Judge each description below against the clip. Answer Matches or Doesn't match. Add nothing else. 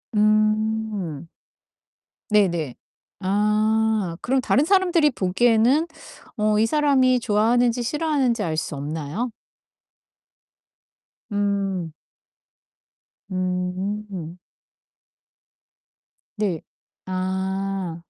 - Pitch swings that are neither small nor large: Matches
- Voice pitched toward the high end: Matches